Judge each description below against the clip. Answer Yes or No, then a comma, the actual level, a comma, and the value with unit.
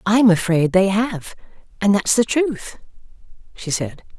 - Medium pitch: No, high, 200 Hz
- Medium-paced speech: Yes, average, 160 wpm